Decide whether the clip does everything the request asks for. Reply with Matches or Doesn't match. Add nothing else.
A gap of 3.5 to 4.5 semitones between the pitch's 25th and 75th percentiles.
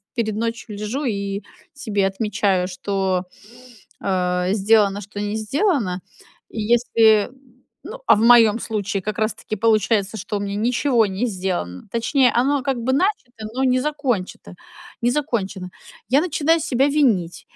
Matches